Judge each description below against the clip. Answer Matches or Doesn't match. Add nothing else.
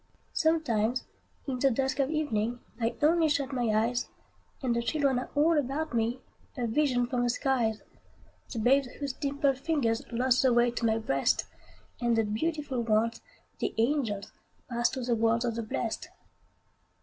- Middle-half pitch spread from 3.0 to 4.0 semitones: Matches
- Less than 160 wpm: Doesn't match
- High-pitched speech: Matches